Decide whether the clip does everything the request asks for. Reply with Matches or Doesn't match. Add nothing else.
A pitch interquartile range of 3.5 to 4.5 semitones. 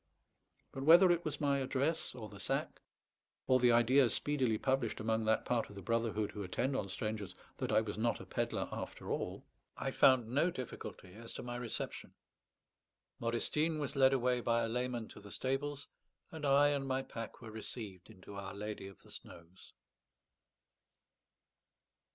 Matches